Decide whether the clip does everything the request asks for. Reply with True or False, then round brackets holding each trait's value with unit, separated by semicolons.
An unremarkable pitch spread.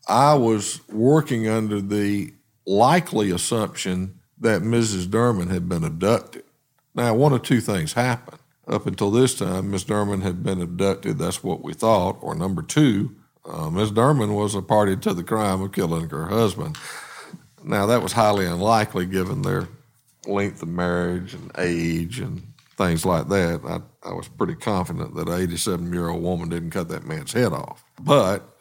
True (4.3 semitones)